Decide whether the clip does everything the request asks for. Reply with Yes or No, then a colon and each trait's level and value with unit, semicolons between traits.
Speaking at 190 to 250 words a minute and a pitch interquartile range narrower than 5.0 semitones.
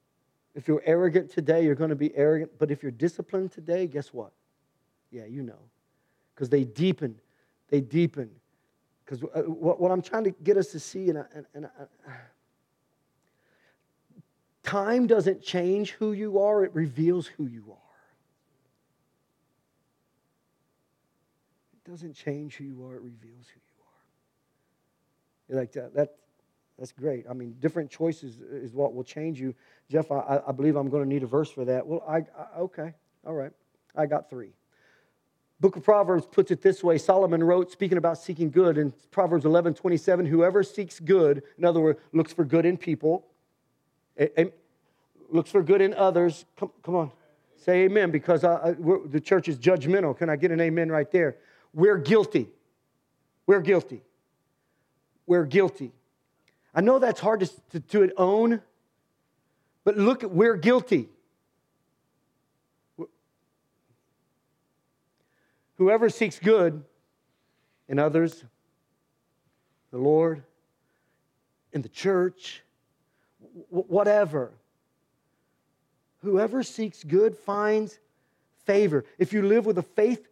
No: average, 145 wpm; average, 4.6 semitones